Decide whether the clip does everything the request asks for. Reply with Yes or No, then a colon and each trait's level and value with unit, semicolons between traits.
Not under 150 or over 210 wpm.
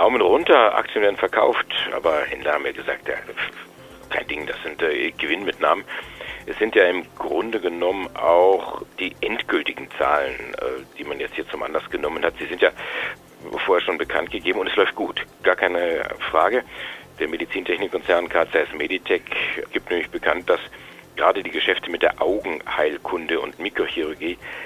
Yes: average, 160 wpm